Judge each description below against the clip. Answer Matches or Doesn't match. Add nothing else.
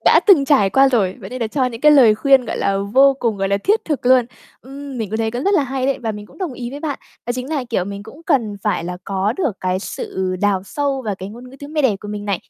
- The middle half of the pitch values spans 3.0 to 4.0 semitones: Doesn't match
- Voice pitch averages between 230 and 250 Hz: Matches